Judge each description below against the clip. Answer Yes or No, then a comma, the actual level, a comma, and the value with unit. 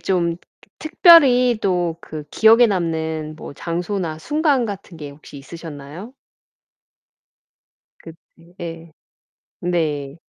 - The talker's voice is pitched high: No, medium, 170 Hz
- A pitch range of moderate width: Yes, average, 5.0 semitones